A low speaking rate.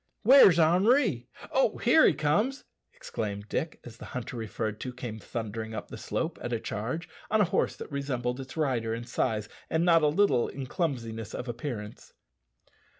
No: average, 175 wpm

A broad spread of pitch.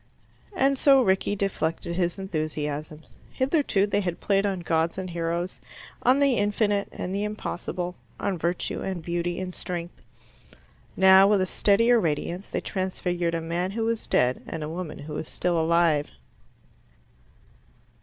No: average, 3.2 semitones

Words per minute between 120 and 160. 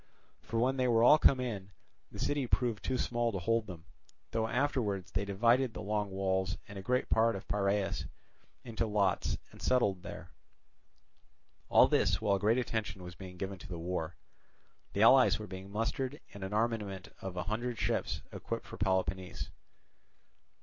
No: average, 170 wpm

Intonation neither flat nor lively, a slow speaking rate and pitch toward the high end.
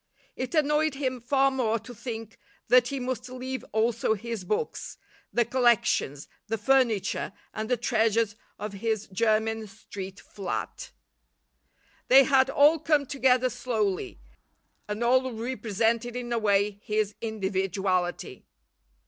Yes: average, 3.5 semitones; slow, 125 wpm; high, 230 Hz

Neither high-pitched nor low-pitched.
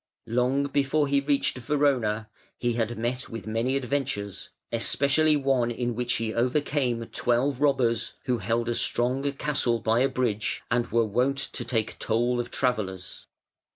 No: low, 125 Hz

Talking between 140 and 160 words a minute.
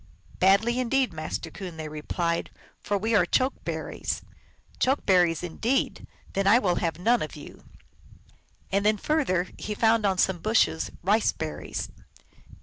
Yes: average, 155 wpm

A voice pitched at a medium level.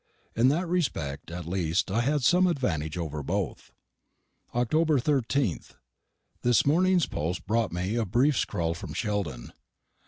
No: low, 115 Hz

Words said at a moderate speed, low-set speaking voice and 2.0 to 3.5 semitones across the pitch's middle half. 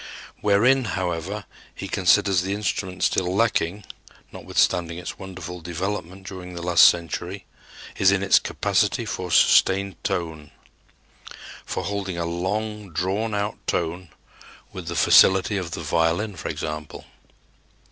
No: slow, 125 wpm; very low, 95 Hz; average, 2.8 semitones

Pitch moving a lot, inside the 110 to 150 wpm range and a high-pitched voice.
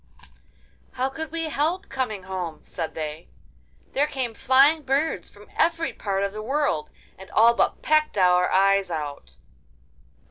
Yes: wide, 8.2 semitones; average, 145 wpm; high, 235 Hz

